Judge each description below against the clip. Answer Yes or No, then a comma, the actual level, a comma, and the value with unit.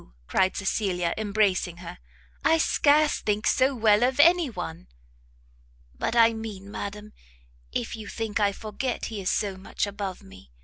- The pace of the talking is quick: No, average, 150 wpm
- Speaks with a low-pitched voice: No, high, 210 Hz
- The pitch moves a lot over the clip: No, average, 3.3 semitones